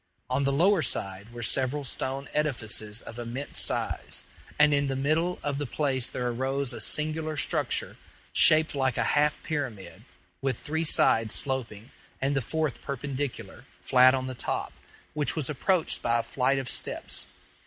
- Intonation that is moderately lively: Yes, average, 3.2 semitones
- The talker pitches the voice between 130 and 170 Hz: Yes, low, 135 Hz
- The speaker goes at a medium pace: Yes, average, 165 wpm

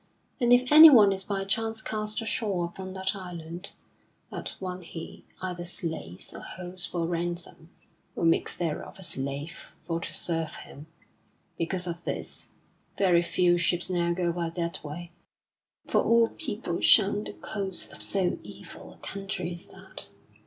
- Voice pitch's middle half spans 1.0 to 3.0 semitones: Yes, narrow, 2.6 semitones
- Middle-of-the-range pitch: Yes, medium, 180 Hz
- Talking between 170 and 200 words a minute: No, average, 155 wpm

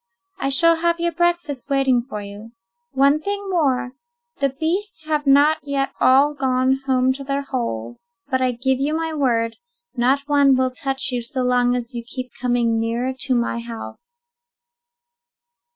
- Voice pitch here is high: Yes, very high, 265 Hz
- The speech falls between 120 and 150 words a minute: No, average, 165 wpm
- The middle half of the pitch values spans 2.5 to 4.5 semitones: Yes, average, 3.0 semitones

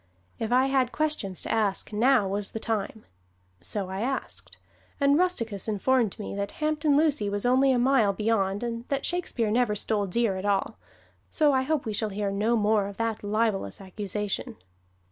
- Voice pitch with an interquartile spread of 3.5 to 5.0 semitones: Yes, average, 4.5 semitones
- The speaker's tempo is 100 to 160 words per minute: No, average, 180 wpm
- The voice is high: Yes, high, 220 Hz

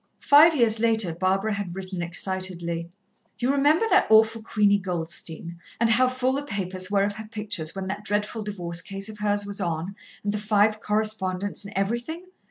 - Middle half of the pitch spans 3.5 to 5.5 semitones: No, average, 2.9 semitones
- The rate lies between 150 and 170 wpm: No, average, 180 wpm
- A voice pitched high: Yes, high, 205 Hz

